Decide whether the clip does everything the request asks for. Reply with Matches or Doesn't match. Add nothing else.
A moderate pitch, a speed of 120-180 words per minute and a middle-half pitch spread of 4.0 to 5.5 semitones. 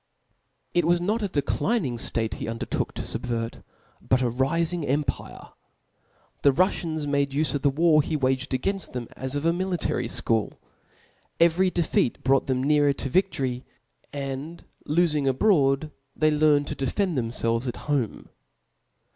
Matches